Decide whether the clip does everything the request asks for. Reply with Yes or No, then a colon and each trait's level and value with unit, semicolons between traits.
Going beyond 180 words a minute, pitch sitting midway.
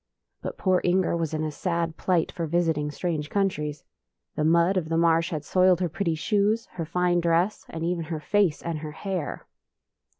Yes: average, 190 wpm; medium, 170 Hz